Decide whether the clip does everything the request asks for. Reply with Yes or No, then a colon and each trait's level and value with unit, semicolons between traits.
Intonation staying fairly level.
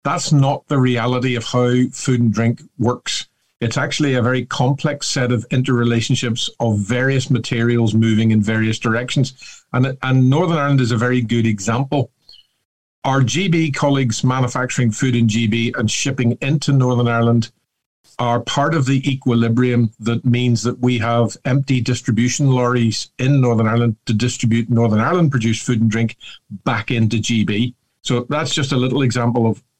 Yes: narrow, 2.3 semitones